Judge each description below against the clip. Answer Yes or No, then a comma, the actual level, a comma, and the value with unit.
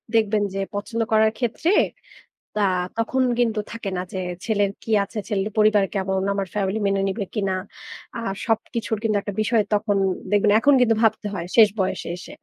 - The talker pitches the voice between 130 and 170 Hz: No, high, 215 Hz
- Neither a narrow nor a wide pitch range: No, narrow, 2.2 semitones